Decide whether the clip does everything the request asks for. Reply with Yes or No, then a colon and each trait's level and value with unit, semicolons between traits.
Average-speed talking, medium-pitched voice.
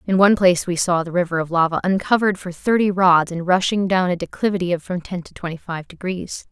No: fast, 230 wpm; medium, 180 Hz